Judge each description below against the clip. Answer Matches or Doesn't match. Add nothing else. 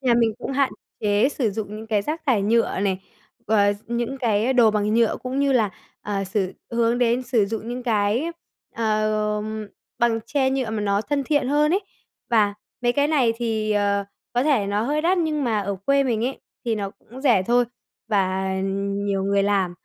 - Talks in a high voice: Matches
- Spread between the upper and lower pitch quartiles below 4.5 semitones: Matches